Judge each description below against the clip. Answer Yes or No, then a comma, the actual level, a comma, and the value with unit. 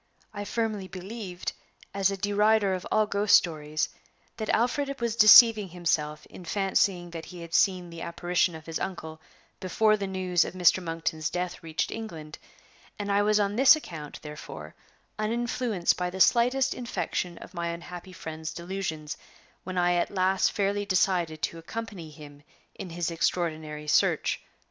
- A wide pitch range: No, average, 3.8 semitones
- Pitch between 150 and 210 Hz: Yes, medium, 185 Hz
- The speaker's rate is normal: Yes, average, 160 wpm